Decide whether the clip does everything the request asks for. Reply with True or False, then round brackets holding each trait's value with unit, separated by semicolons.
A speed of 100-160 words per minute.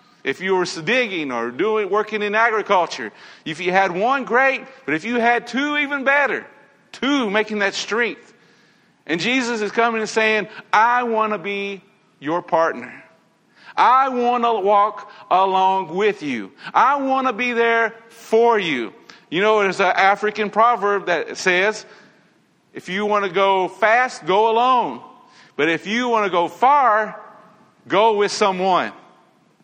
True (155 wpm)